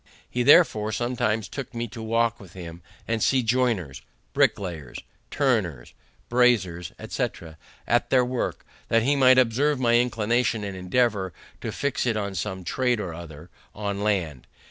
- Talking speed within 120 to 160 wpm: Yes, average, 150 wpm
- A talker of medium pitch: No, low, 110 Hz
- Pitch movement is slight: No, average, 5.0 semitones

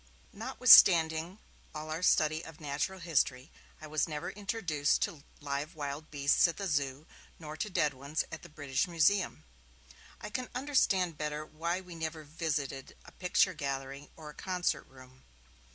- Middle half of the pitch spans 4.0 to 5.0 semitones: No, average, 3.3 semitones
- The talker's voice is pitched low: No, medium, 155 Hz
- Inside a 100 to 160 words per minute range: Yes, average, 155 wpm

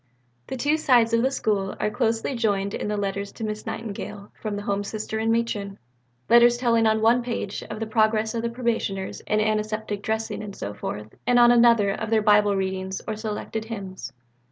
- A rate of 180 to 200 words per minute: Yes, average, 195 wpm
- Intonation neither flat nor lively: No, narrow, 2.2 semitones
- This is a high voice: Yes, high, 215 Hz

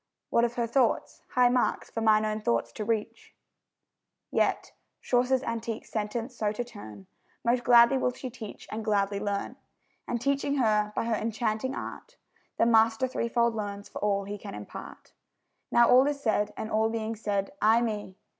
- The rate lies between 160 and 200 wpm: Yes, average, 175 wpm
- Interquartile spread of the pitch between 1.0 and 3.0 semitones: Yes, narrow, 2.4 semitones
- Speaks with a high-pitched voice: Yes, high, 225 Hz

